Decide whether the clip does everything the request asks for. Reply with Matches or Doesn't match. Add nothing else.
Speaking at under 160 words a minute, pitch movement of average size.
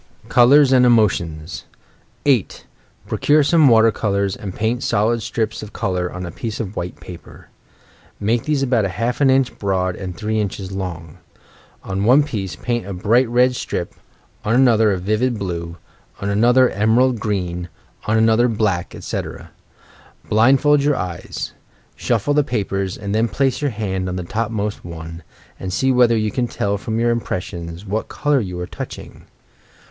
Doesn't match